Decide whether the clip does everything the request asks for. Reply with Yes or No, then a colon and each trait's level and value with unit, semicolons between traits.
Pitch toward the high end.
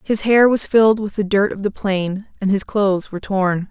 Yes: high, 200 Hz